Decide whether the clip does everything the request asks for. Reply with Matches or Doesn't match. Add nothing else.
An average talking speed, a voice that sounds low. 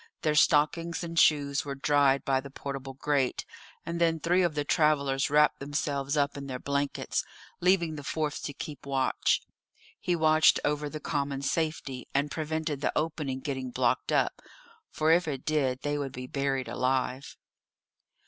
Doesn't match